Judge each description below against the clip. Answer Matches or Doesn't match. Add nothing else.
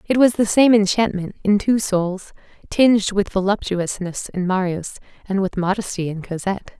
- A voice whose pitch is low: Doesn't match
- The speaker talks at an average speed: Matches